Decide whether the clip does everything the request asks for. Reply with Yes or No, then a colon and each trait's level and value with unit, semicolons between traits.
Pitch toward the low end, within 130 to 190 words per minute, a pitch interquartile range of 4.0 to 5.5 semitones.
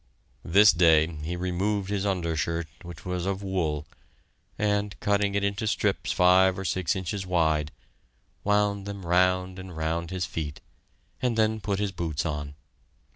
No: very low, 90 Hz; average, 150 wpm; average, 3.2 semitones